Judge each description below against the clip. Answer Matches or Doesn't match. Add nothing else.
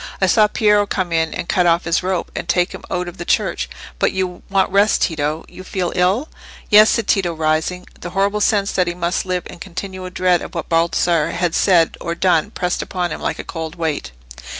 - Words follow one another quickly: Matches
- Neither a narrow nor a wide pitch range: Doesn't match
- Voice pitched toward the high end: Doesn't match